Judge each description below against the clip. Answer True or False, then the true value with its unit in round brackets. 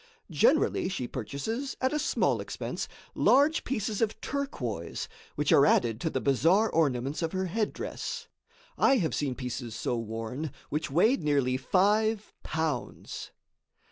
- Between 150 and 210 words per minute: False (140 wpm)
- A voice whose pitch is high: False (160 Hz)